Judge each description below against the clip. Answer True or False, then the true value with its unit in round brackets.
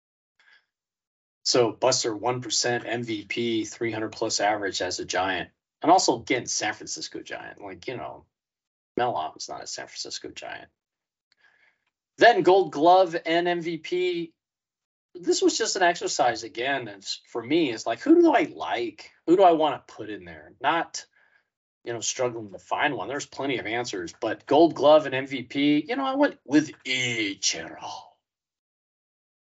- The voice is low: False (150 Hz)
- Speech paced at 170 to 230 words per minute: False (155 wpm)